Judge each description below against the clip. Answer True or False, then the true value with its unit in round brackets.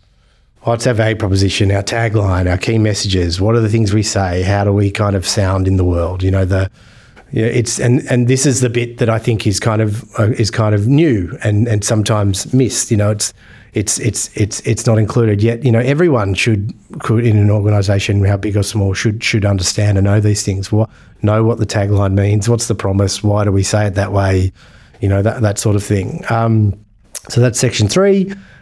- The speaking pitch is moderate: False (105 Hz)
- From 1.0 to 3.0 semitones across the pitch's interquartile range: True (2.5 semitones)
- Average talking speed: False (230 wpm)